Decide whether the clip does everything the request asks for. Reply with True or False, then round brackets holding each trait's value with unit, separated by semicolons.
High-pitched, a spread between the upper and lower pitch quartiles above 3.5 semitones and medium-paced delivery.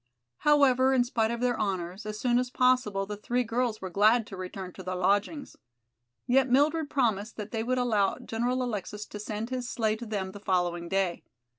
True (220 Hz; 4.1 semitones; 195 wpm)